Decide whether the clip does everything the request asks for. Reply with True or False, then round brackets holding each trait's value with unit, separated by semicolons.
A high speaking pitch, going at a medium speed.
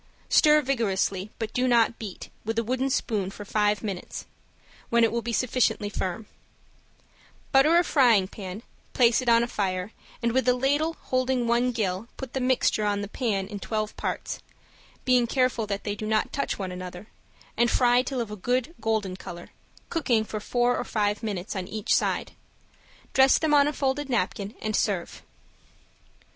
True (230 Hz; 180 wpm)